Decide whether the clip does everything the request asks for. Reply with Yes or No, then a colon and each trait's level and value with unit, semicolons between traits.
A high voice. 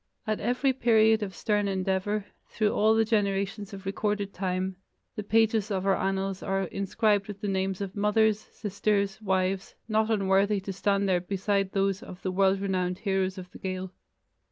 Yes: high, 195 Hz